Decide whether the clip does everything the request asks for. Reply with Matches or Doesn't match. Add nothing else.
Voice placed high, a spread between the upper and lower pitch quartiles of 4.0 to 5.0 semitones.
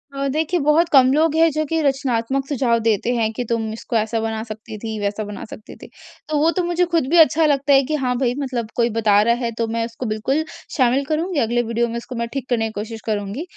Matches